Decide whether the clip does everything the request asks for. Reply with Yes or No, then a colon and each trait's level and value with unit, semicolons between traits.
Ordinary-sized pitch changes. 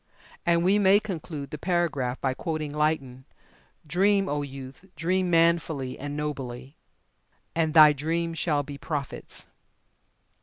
Yes: average, 3.3 semitones